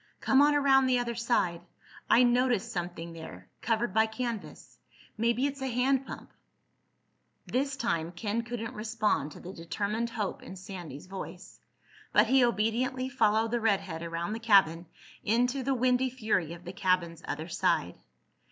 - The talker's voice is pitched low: No, high, 225 Hz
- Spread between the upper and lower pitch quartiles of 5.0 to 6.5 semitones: Yes, average, 5.3 semitones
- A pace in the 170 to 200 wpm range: No, average, 150 wpm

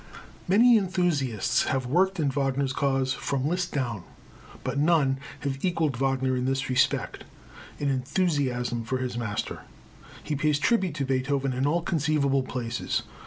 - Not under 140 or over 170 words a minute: Yes, average, 145 wpm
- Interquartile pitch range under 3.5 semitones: Yes, average, 3.1 semitones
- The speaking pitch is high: No, low, 135 Hz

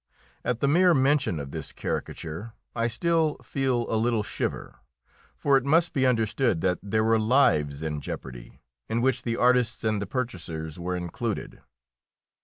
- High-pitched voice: No, low, 115 Hz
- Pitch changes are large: Yes, wide, 7.0 semitones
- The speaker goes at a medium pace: Yes, average, 160 wpm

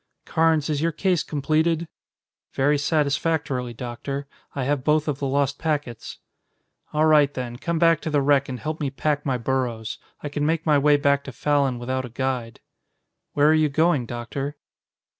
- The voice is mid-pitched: Yes, medium, 145 Hz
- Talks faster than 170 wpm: Yes, average, 180 wpm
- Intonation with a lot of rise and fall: No, average, 2.8 semitones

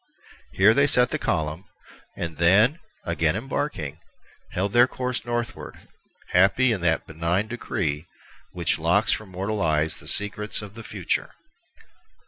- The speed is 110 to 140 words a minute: Yes, slow, 135 wpm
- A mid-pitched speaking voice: No, very low, 95 Hz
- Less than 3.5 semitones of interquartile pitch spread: No, wide, 5.6 semitones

